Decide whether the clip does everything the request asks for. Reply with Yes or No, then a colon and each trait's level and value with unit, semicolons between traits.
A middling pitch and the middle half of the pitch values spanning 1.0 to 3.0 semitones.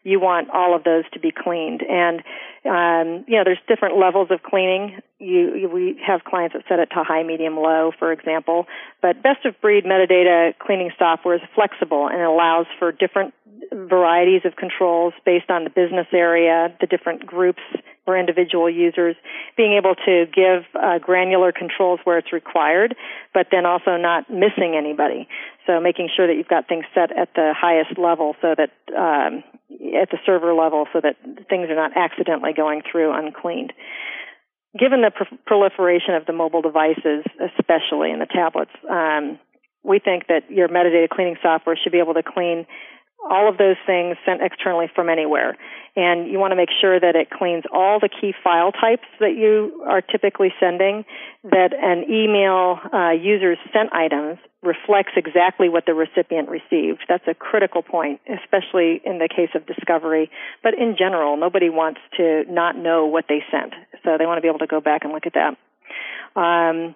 Yes: medium, 175 Hz; narrow, 2.4 semitones